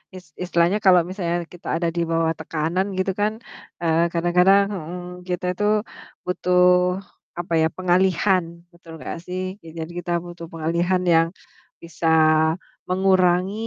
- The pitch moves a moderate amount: No, narrow, 1.6 semitones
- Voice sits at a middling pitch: Yes, medium, 180 Hz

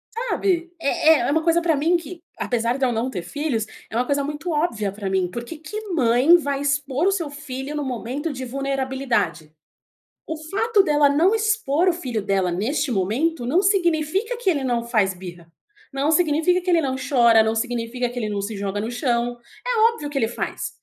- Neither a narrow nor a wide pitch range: No, wide, 5.8 semitones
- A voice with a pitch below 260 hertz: No, very high, 275 Hz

